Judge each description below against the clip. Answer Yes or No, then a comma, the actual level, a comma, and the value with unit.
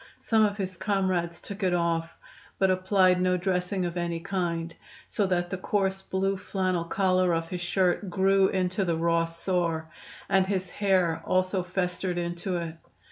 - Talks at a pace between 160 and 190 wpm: Yes, average, 165 wpm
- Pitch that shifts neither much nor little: No, narrow, 1.9 semitones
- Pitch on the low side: No, medium, 185 Hz